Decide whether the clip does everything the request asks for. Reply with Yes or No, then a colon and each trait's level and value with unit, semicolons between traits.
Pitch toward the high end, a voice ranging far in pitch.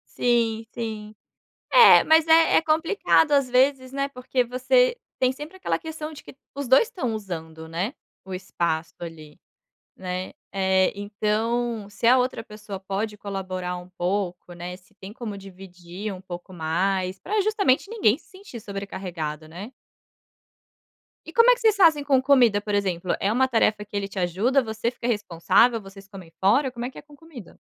Yes: high, 215 Hz; wide, 5.8 semitones